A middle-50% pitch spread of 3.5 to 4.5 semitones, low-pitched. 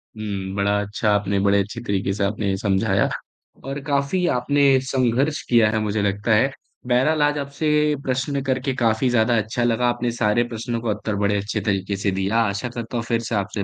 Yes: average, 4.0 semitones; low, 115 Hz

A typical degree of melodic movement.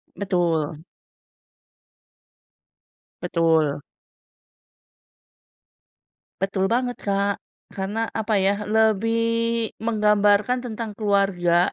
Yes: average, 3.0 semitones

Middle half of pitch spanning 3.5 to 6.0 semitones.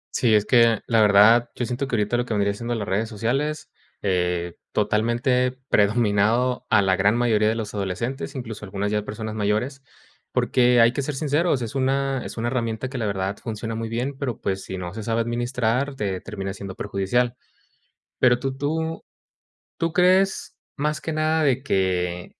Yes: average, 4.0 semitones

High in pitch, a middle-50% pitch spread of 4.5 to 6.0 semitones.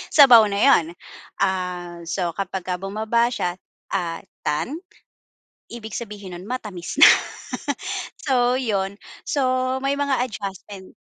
Yes: high, 200 Hz; average, 4.8 semitones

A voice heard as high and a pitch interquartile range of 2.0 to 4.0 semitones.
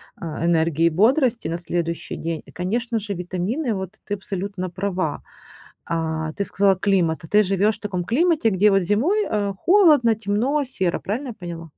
No: high, 195 Hz; average, 4.5 semitones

